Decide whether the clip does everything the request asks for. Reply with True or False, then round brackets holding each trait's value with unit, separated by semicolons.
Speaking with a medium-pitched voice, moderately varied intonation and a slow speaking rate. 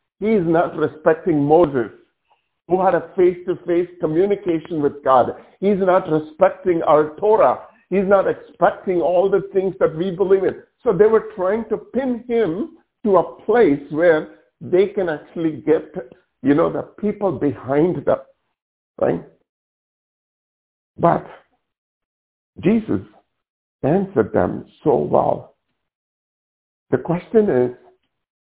True (180 Hz; 4.4 semitones; 120 wpm)